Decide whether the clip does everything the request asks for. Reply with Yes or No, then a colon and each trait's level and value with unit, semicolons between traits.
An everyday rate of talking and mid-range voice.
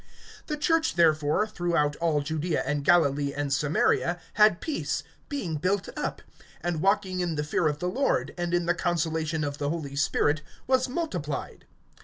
Yes: average, 165 wpm; medium, 170 Hz